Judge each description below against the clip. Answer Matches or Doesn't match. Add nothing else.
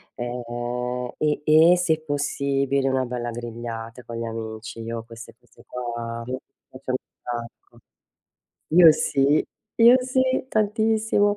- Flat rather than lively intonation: Doesn't match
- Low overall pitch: Matches